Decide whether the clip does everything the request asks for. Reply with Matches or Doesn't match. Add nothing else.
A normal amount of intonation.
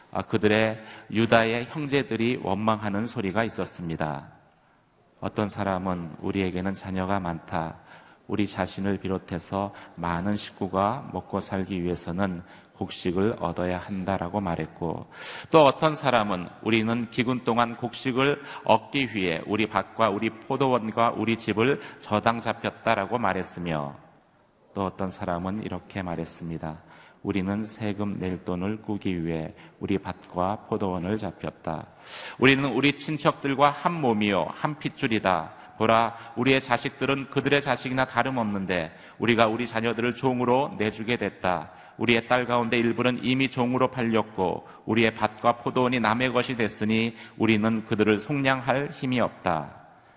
Matches